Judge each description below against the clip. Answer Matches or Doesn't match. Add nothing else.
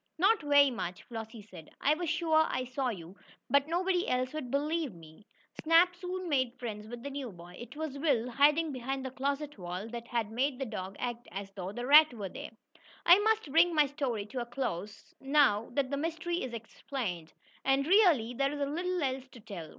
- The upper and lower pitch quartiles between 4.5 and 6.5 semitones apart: Matches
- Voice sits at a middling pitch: Doesn't match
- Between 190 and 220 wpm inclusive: Matches